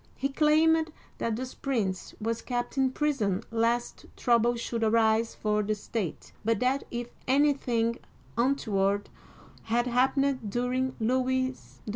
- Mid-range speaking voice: No, high, 240 Hz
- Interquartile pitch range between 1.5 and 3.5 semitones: Yes, average, 2.7 semitones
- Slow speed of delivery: Yes, slow, 130 wpm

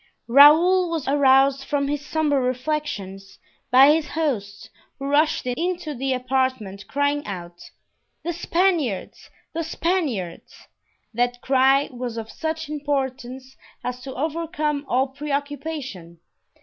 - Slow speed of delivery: Yes, slow, 115 wpm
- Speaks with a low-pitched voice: No, very high, 275 Hz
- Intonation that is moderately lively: Yes, average, 3.4 semitones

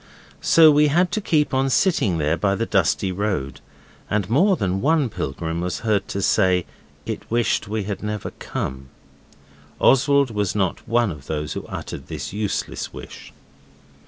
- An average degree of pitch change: No, wide, 6.9 semitones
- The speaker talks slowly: No, average, 160 wpm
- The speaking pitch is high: No, low, 105 Hz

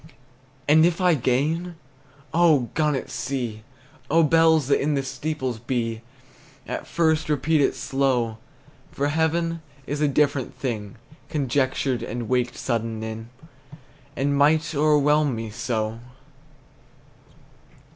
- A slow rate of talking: Yes, slow, 120 wpm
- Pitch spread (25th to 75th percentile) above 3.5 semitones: Yes, average, 4.3 semitones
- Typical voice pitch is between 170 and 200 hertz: No, medium, 140 Hz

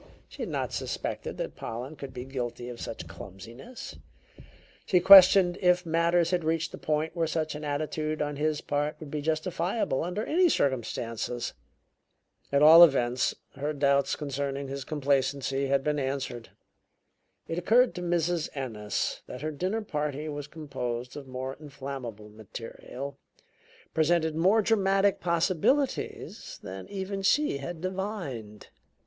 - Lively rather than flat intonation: No, average, 4.6 semitones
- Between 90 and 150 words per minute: Yes, average, 140 wpm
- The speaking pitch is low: No, medium, 150 Hz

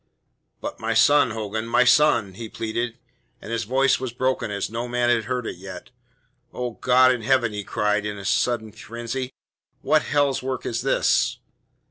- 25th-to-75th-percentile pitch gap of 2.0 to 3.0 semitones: Yes, average, 2.7 semitones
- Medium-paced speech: Yes, average, 175 wpm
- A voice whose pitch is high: No, low, 120 Hz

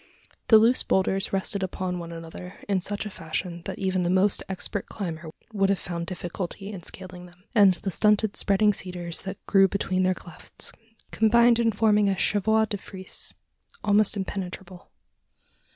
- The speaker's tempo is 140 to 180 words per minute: Yes, average, 160 wpm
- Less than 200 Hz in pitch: Yes, high, 190 Hz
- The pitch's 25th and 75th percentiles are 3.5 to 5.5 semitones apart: No, narrow, 2.4 semitones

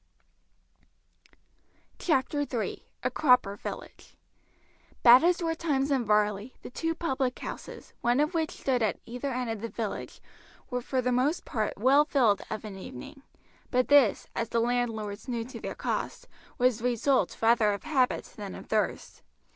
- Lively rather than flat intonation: No, average, 3.5 semitones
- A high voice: Yes, very high, 250 Hz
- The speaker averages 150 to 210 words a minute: Yes, average, 165 wpm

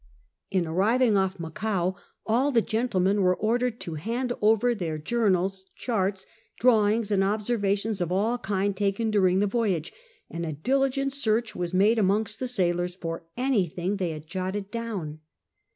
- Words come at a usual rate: Yes, average, 160 wpm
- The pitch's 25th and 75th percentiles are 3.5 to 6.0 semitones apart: Yes, average, 3.9 semitones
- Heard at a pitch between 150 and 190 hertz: No, high, 200 Hz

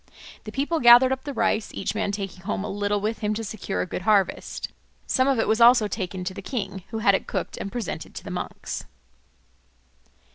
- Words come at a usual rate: No, fast, 215 wpm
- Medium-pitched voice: No, high, 215 Hz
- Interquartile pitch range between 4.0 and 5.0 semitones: No, average, 3.4 semitones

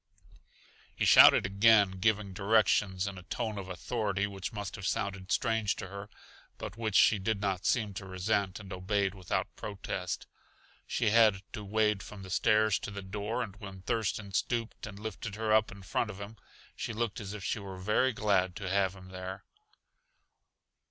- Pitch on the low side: Yes, low, 100 Hz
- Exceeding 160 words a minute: Yes, average, 180 wpm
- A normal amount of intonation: No, narrow, 2.2 semitones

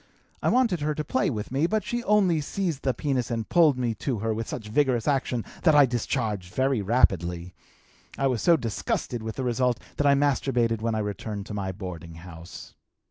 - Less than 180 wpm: No, average, 200 wpm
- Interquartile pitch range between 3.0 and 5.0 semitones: No, wide, 5.4 semitones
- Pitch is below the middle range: Yes, low, 125 Hz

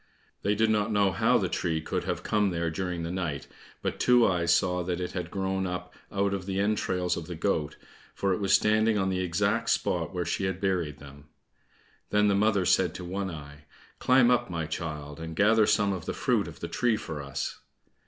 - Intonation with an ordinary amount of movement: Yes, average, 3.3 semitones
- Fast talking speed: Yes, fast, 215 wpm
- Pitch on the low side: Yes, very low, 95 Hz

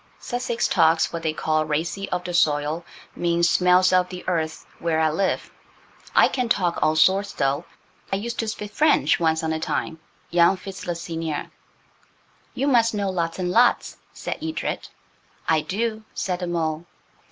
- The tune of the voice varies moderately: Yes, average, 3.6 semitones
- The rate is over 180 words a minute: No, average, 165 wpm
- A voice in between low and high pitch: Yes, medium, 175 Hz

